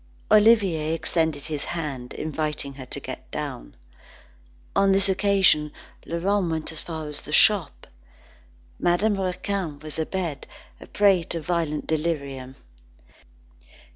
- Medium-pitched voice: Yes, medium, 160 Hz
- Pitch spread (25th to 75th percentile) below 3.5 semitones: No, average, 4.1 semitones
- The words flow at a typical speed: No, slow, 120 wpm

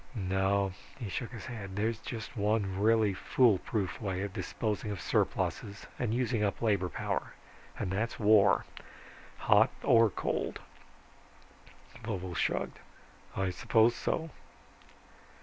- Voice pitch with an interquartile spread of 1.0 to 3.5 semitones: Yes, average, 2.9 semitones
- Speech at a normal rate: No, slow, 120 wpm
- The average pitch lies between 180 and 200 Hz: No, low, 105 Hz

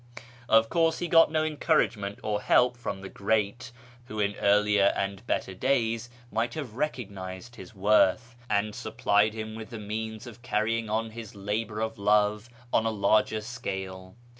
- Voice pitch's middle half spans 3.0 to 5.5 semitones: No, narrow, 2.4 semitones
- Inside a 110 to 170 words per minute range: Yes, average, 165 wpm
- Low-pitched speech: Yes, low, 110 Hz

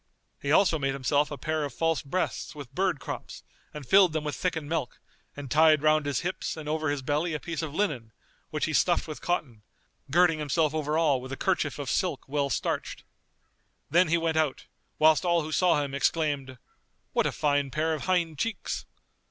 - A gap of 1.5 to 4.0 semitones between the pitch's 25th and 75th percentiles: Yes, narrow, 2.5 semitones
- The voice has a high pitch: No, medium, 155 Hz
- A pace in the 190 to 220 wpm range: Yes, average, 200 wpm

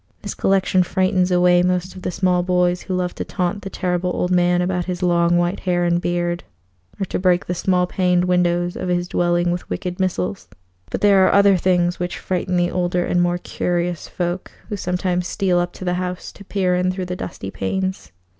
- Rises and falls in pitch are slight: Yes, narrow, 0.8 semitones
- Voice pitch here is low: No, medium, 180 Hz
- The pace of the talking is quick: Yes, fast, 210 wpm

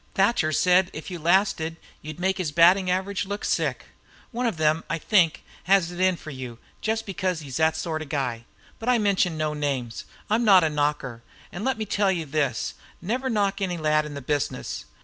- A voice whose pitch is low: No, medium, 170 Hz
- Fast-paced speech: Yes, fast, 210 wpm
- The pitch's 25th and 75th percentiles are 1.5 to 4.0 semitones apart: No, average, 4.4 semitones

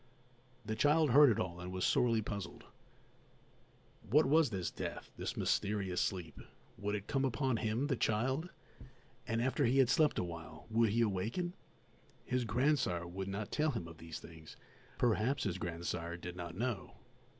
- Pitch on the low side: Yes, low, 110 Hz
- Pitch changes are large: Yes, wide, 6.5 semitones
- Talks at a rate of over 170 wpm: No, average, 160 wpm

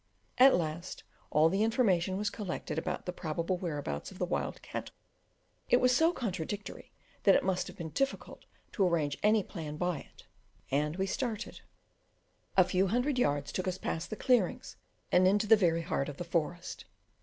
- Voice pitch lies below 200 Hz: Yes, medium, 185 Hz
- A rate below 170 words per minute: No, average, 180 wpm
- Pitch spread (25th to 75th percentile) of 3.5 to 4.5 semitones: Yes, average, 4.2 semitones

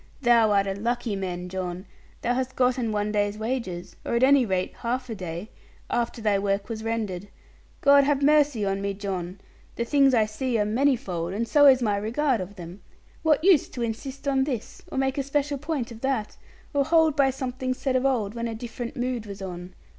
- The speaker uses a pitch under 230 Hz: No, high, 235 Hz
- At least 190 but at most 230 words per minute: Yes, fast, 205 wpm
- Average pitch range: Yes, average, 4.9 semitones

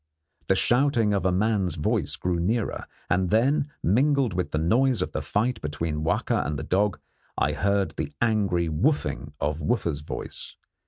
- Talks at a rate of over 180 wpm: No, average, 165 wpm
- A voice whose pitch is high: No, very low, 95 Hz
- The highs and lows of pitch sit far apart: Yes, wide, 5.9 semitones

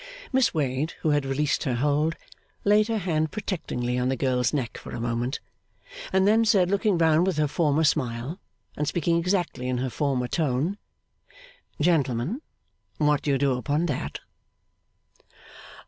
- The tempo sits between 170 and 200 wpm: No, average, 155 wpm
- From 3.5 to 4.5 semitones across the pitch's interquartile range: No, average, 5.1 semitones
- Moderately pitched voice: Yes, medium, 150 Hz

